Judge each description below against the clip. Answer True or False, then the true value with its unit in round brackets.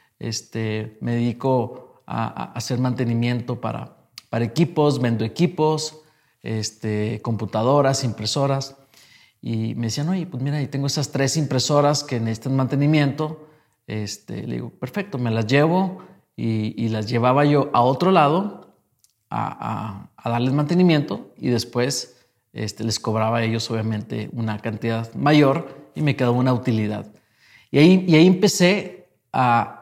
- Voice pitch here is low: True (125 Hz)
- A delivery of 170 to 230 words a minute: False (145 wpm)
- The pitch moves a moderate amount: True (4.5 semitones)